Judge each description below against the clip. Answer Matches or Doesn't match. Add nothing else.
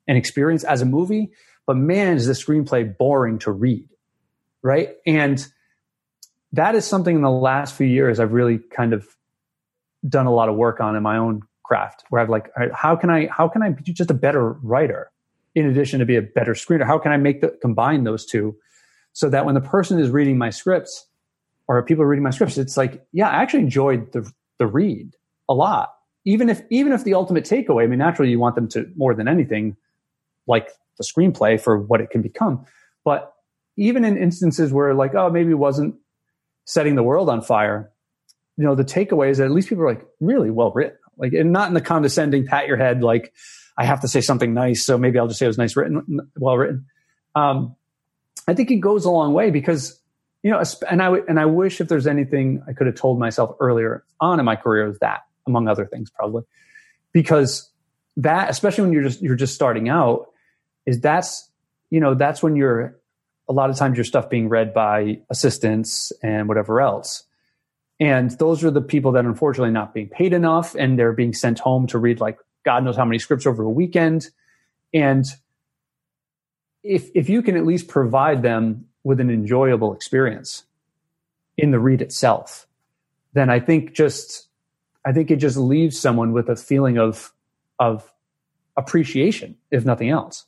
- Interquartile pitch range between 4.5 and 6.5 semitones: Matches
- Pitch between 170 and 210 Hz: Doesn't match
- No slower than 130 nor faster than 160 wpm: Doesn't match